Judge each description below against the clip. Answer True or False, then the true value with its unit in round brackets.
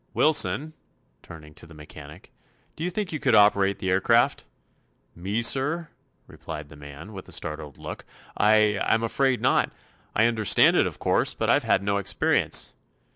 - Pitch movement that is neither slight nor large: False (6.6 semitones)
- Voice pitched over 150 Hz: False (105 Hz)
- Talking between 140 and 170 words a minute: True (160 wpm)